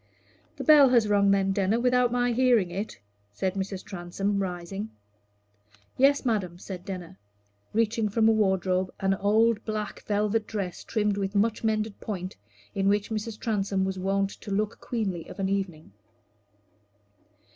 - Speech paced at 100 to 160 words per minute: Yes, average, 150 wpm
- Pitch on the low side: No, high, 200 Hz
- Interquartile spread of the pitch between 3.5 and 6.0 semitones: No, narrow, 2.4 semitones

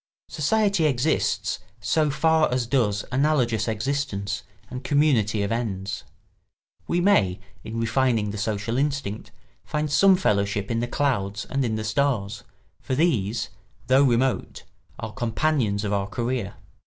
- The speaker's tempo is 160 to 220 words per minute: No, slow, 135 wpm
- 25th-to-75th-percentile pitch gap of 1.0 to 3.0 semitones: No, wide, 5.4 semitones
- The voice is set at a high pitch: No, low, 120 Hz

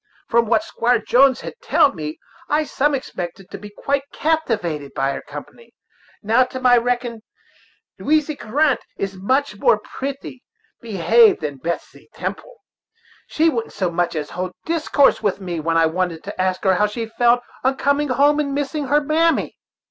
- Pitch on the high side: Yes, high, 240 Hz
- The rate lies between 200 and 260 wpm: No, average, 170 wpm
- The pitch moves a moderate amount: No, wide, 7.3 semitones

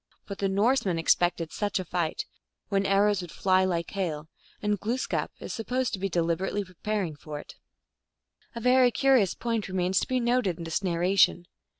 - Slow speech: No, average, 175 wpm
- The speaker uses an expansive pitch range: No, average, 3.5 semitones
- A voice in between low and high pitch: No, high, 195 Hz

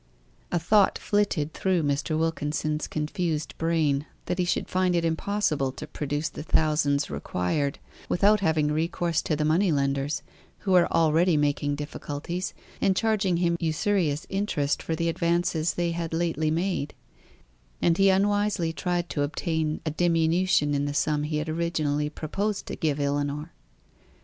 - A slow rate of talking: No, average, 150 wpm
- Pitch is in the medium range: Yes, medium, 160 Hz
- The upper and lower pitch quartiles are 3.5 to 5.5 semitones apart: No, average, 2.9 semitones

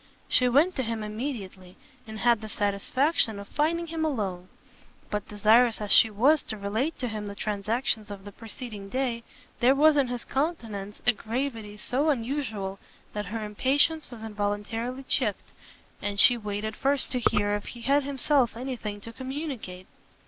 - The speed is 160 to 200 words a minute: Yes, average, 170 wpm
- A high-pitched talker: Yes, high, 230 Hz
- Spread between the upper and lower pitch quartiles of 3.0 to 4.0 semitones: No, average, 4.4 semitones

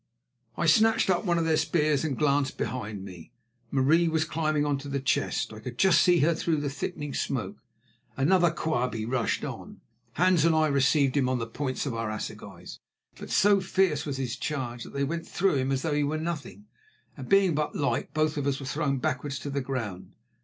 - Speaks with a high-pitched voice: No, medium, 145 Hz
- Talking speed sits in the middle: No, fast, 210 wpm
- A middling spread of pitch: Yes, average, 3.7 semitones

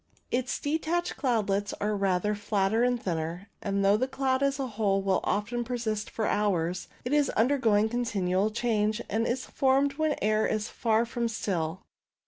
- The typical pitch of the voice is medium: No, high, 220 Hz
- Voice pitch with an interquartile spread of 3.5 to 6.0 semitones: Yes, average, 3.8 semitones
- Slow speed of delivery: No, average, 175 wpm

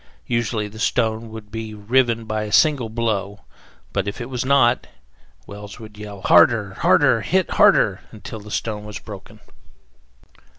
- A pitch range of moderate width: No, narrow, 2.2 semitones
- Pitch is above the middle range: No, low, 110 Hz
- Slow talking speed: No, average, 155 wpm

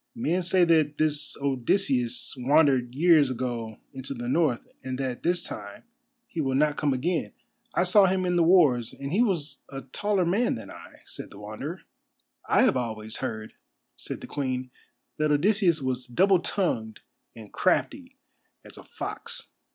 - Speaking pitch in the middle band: Yes, medium, 145 Hz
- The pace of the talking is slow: No, average, 165 wpm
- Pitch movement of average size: No, wide, 5.7 semitones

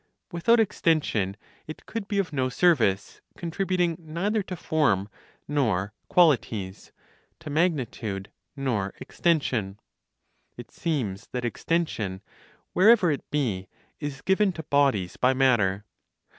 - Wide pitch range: Yes, wide, 8.3 semitones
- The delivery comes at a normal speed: No, slow, 115 wpm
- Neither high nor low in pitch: Yes, medium, 145 Hz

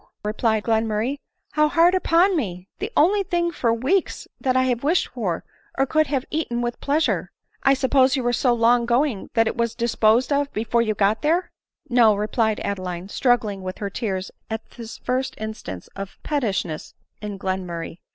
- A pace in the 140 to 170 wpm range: No, average, 190 wpm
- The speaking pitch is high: Yes, high, 235 Hz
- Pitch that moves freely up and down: No, average, 4.9 semitones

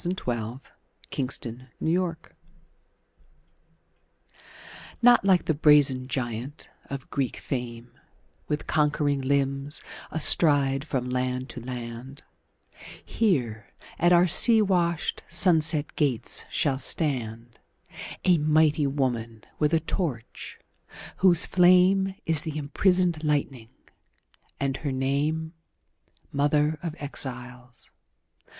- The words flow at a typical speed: No, slow, 90 wpm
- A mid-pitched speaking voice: Yes, medium, 145 Hz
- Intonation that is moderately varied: Yes, average, 4.1 semitones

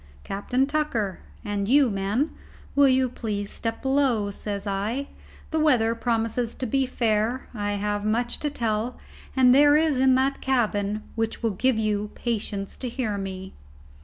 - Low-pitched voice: No, high, 230 Hz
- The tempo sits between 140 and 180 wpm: Yes, average, 155 wpm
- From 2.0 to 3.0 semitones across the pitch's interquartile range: No, average, 4.1 semitones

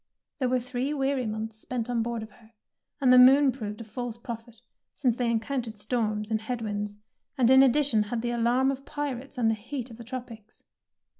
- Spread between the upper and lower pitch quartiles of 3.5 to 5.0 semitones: No, narrow, 2.6 semitones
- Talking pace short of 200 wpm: No, fast, 205 wpm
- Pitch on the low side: No, high, 240 Hz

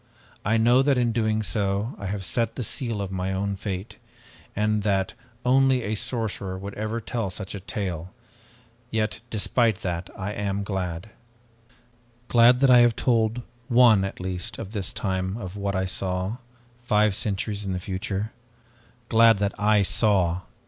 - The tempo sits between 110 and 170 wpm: Yes, average, 165 wpm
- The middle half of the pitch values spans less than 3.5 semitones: Yes, average, 3.0 semitones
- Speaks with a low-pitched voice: Yes, low, 105 Hz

